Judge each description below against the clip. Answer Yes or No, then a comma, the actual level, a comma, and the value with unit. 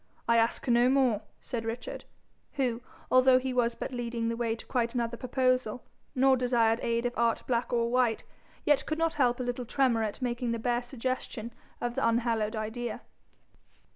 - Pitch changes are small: Yes, narrow, 1.6 semitones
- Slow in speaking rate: No, average, 180 wpm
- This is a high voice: Yes, high, 240 Hz